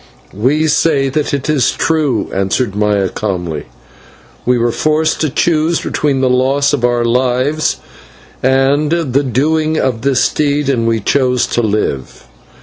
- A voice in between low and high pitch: No, low, 130 Hz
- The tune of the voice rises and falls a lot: No, average, 4.1 semitones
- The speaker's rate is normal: Yes, average, 145 wpm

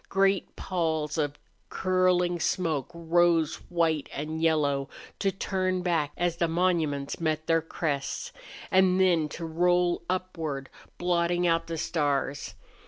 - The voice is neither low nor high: Yes, medium, 170 Hz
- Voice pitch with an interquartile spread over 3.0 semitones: No, narrow, 2.5 semitones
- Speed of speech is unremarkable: No, slow, 125 wpm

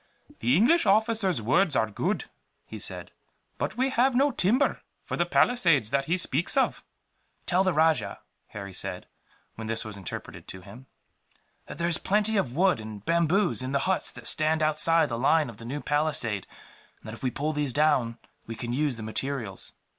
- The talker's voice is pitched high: No, medium, 150 Hz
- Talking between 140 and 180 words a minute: No, average, 190 wpm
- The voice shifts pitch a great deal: Yes, wide, 8.1 semitones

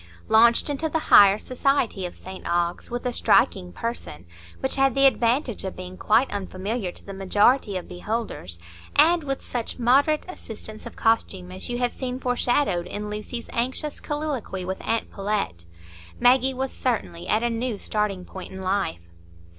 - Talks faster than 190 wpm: No, average, 165 wpm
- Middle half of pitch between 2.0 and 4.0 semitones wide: No, average, 5.1 semitones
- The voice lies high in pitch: Yes, high, 225 Hz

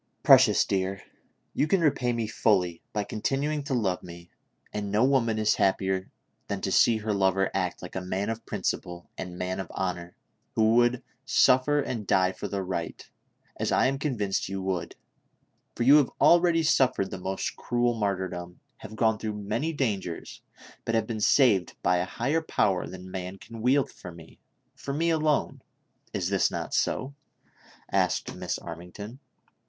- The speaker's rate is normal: Yes, average, 175 wpm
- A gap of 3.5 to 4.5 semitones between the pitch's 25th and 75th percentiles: No, wide, 5.4 semitones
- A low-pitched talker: Yes, low, 105 Hz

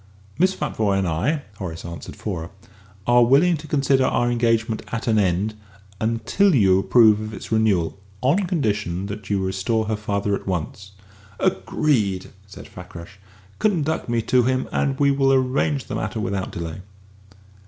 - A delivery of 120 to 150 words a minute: No, average, 160 wpm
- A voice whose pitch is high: No, low, 110 Hz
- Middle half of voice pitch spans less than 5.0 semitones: No, wide, 5.5 semitones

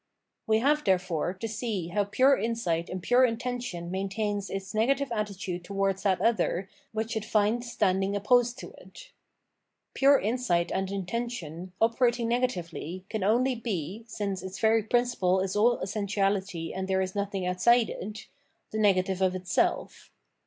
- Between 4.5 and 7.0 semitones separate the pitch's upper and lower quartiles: No, average, 3.8 semitones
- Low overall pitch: No, high, 205 Hz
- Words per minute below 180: Yes, average, 155 wpm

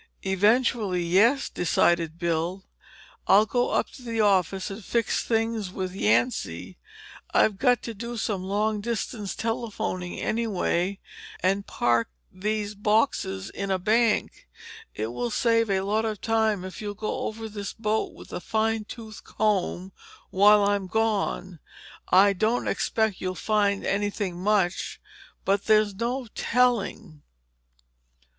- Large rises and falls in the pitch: No, average, 3.0 semitones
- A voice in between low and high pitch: No, high, 205 Hz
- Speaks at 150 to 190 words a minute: No, slow, 135 wpm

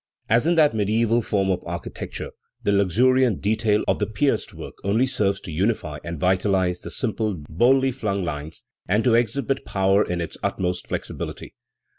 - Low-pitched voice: Yes, low, 105 Hz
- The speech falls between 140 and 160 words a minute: No, average, 170 wpm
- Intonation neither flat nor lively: Yes, average, 4.2 semitones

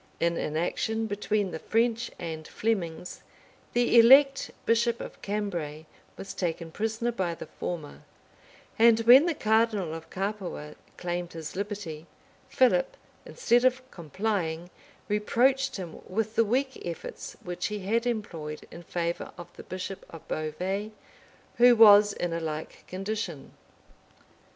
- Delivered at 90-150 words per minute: Yes, slow, 135 wpm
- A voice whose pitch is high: Yes, high, 200 Hz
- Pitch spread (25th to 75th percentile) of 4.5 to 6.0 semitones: Yes, average, 5.1 semitones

